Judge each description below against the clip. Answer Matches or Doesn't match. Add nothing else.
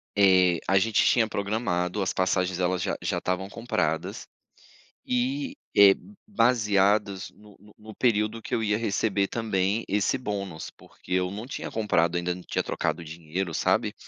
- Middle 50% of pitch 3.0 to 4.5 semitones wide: Matches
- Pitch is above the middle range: Doesn't match